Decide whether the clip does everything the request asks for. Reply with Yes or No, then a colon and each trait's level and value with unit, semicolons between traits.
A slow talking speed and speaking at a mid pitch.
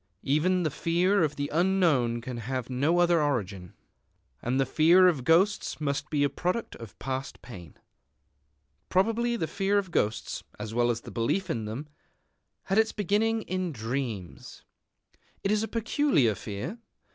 No: average, 155 wpm; medium, 155 Hz